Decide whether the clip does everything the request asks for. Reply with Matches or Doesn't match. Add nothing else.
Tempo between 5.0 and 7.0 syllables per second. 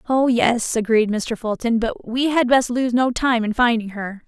Doesn't match